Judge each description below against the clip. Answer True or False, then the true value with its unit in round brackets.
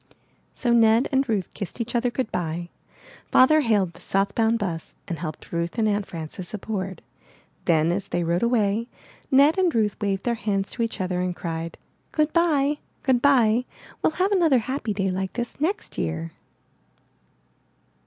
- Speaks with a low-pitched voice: False (215 Hz)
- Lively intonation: True (5.8 semitones)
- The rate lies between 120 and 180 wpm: True (165 wpm)